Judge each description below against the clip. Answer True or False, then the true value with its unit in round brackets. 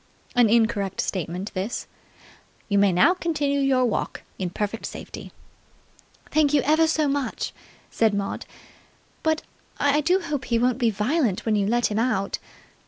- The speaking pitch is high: True (240 Hz)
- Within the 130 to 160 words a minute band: True (155 wpm)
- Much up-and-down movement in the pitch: True (5.9 semitones)